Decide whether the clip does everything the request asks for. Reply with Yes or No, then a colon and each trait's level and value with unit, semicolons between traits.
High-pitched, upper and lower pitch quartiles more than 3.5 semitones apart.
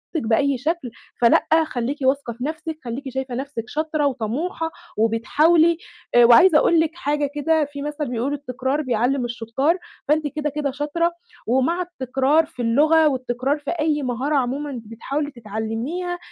Yes: very high, 280 Hz; average, 3.9 semitones